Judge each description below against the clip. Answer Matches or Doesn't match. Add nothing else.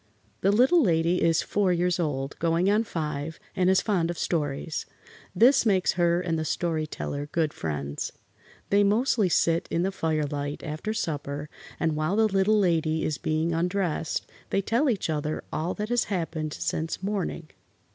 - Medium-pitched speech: Matches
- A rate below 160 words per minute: Doesn't match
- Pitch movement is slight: Doesn't match